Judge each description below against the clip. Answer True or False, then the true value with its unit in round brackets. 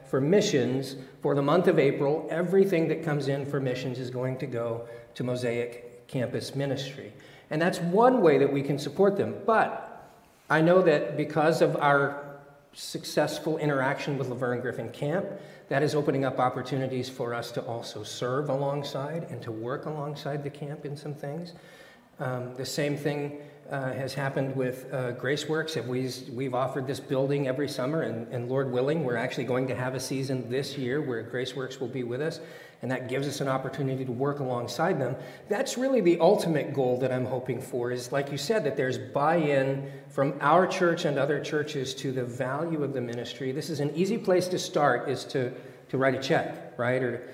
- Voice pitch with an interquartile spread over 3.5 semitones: False (2.9 semitones)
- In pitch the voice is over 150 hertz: False (140 Hz)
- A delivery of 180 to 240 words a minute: True (190 wpm)